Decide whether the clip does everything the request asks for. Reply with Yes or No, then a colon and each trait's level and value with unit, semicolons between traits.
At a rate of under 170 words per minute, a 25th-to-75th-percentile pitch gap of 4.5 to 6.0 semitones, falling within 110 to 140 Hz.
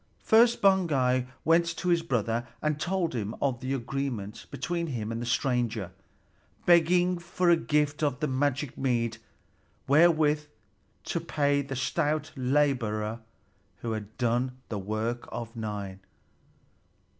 Yes: slow, 135 wpm; average, 5.1 semitones; low, 135 Hz